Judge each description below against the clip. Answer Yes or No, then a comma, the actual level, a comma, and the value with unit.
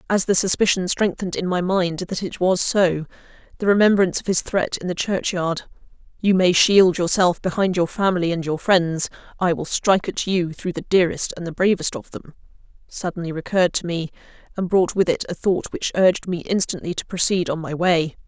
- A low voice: No, medium, 180 Hz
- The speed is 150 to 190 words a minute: No, average, 200 wpm